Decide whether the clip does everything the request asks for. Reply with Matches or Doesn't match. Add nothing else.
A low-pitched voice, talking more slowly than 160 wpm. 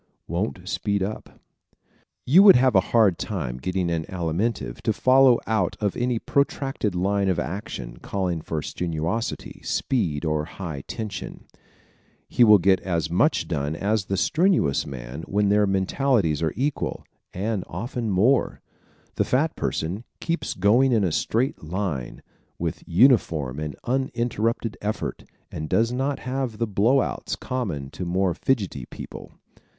Matches